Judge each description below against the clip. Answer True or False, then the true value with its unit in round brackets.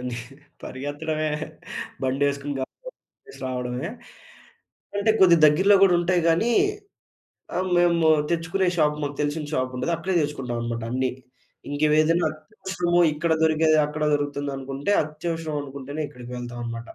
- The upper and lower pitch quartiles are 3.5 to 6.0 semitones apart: True (4.0 semitones)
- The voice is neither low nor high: True (150 Hz)